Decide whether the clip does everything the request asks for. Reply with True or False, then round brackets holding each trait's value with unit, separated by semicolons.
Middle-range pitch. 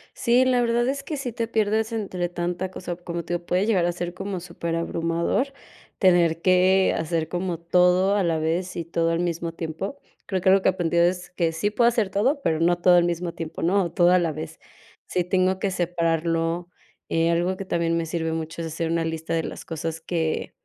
True (175 Hz)